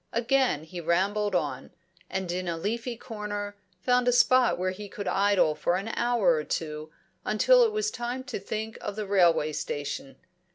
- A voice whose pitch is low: No, high, 205 Hz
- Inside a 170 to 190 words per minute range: Yes, average, 175 wpm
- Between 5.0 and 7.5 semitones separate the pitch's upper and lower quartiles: Yes, wide, 5.4 semitones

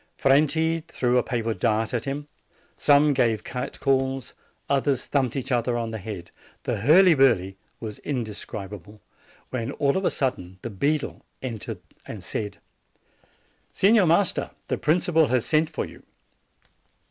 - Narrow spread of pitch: No, average, 4.8 semitones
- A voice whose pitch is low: Yes, low, 130 Hz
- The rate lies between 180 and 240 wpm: No, average, 145 wpm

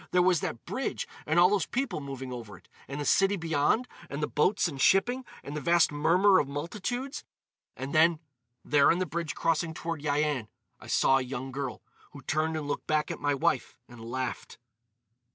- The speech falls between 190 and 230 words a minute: Yes, average, 195 wpm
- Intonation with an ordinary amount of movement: Yes, average, 4.0 semitones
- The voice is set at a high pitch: No, medium, 150 Hz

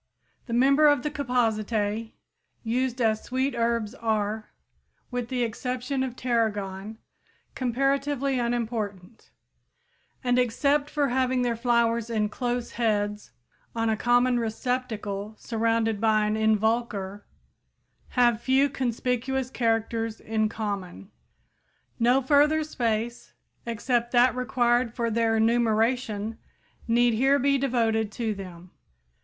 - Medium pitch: No, high, 235 Hz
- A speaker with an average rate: No, slow, 115 wpm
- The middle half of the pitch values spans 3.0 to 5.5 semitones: No, narrow, 2.4 semitones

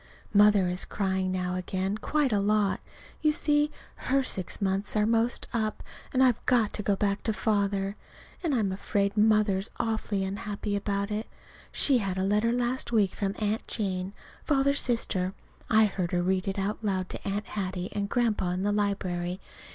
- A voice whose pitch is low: No, high, 205 Hz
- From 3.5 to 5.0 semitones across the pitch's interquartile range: No, narrow, 2.5 semitones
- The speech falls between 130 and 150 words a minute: No, average, 180 wpm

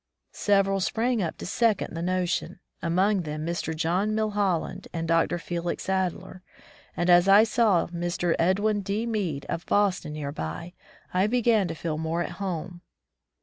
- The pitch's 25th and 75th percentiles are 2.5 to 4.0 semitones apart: Yes, average, 3.4 semitones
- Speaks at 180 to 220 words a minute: No, average, 160 wpm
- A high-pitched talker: No, medium, 180 Hz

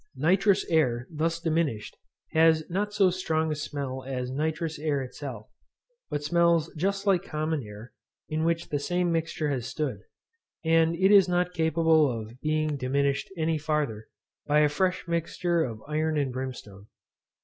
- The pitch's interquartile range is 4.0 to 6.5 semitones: No, average, 3.4 semitones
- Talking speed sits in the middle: Yes, average, 155 wpm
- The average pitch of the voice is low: No, medium, 155 Hz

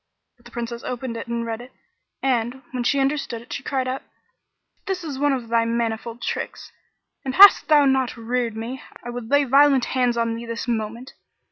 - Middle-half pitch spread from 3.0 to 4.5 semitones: No, narrow, 2.5 semitones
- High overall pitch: Yes, high, 245 Hz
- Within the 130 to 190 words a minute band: No, average, 200 wpm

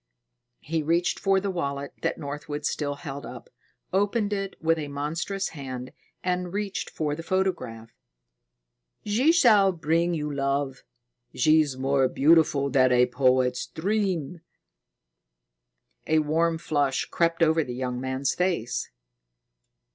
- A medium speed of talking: No, slow, 125 wpm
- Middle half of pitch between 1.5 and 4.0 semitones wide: No, average, 4.5 semitones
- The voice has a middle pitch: Yes, medium, 155 Hz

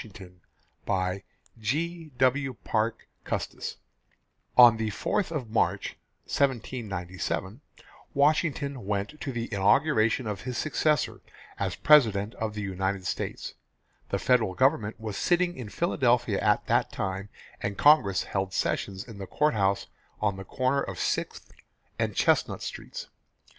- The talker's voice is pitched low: Yes, low, 110 Hz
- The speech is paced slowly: Yes, slow, 125 wpm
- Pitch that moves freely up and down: Yes, wide, 5.8 semitones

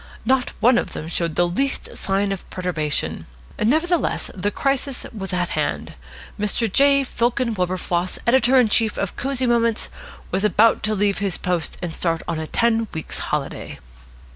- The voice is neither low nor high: No, high, 210 Hz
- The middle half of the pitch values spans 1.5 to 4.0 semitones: No, average, 5.3 semitones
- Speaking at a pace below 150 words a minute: No, average, 165 wpm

